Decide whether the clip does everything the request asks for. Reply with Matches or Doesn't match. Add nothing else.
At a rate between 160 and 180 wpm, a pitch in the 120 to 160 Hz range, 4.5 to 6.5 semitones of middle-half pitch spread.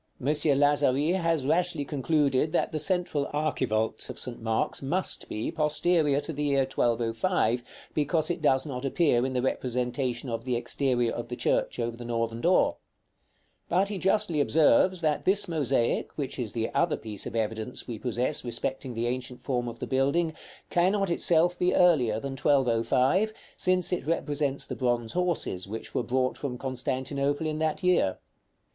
Matches